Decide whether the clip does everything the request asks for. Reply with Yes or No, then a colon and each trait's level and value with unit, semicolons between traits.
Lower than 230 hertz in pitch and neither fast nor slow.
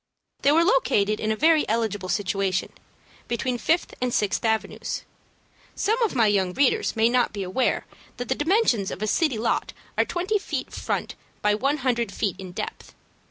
No: high, 235 Hz; average, 180 wpm